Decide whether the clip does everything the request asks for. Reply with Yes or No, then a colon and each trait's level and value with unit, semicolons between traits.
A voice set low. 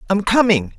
No: high, 225 Hz